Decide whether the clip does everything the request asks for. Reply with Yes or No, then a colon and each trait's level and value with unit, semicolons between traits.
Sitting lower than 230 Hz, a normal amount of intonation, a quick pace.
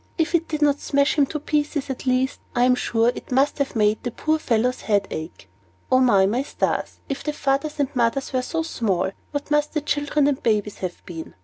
No: very high, 265 Hz; average, 4.4 semitones; fast, 230 wpm